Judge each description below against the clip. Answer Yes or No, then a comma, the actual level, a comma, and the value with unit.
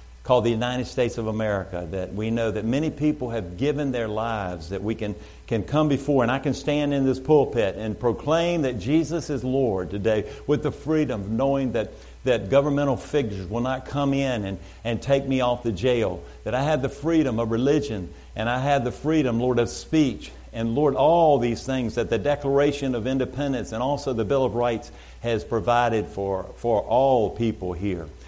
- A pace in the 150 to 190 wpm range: No, average, 200 wpm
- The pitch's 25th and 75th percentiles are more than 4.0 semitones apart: Yes, average, 4.4 semitones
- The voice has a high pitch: No, low, 120 Hz